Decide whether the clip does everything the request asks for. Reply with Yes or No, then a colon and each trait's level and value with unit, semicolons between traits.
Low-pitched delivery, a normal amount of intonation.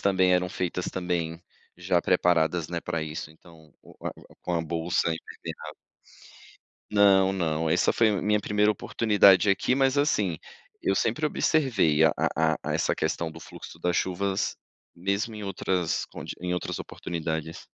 Yes: very low, 90 Hz; average, 3.4 semitones